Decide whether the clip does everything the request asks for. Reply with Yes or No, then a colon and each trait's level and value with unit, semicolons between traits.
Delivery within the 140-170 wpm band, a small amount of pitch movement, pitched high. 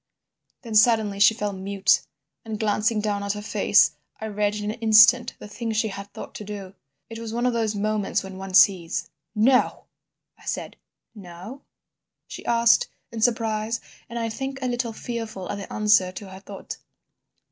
No: average, 180 wpm; narrow, 2.3 semitones; high, 215 Hz